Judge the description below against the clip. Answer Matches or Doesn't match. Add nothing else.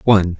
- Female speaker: Doesn't match